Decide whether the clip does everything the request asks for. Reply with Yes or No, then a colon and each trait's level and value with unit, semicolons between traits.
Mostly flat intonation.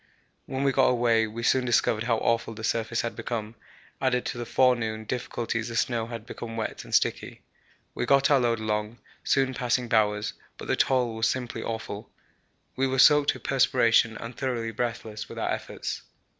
Yes: narrow, 2.1 semitones